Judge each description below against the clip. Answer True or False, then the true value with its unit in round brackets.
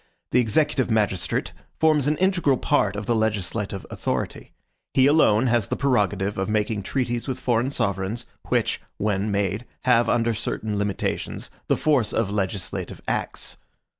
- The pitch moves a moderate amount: True (3.9 semitones)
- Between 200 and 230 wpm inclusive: False (145 wpm)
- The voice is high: False (110 Hz)